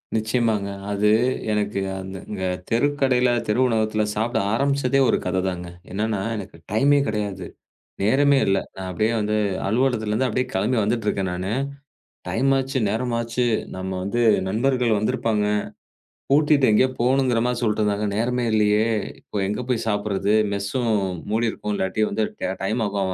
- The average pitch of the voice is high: No, low, 110 Hz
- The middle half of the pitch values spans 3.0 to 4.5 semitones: Yes, average, 3.5 semitones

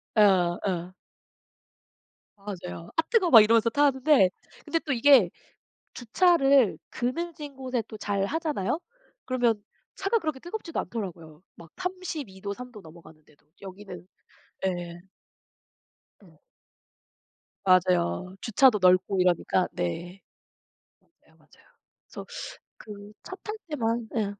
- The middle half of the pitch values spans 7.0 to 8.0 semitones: Yes, wide, 7.4 semitones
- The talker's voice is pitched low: No, high, 215 Hz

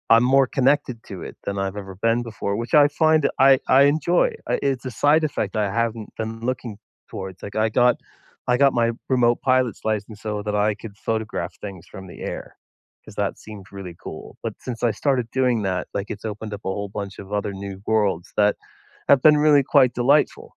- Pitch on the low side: Yes, low, 115 Hz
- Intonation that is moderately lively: Yes, average, 4.2 semitones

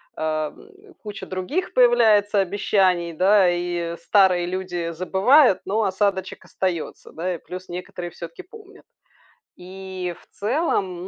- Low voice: No, medium, 185 Hz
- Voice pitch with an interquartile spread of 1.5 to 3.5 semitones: Yes, average, 2.9 semitones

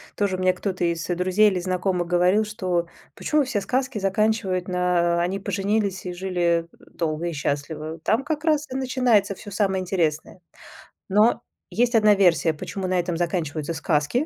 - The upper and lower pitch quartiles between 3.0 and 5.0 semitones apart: Yes, average, 3.4 semitones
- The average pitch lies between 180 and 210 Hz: Yes, medium, 185 Hz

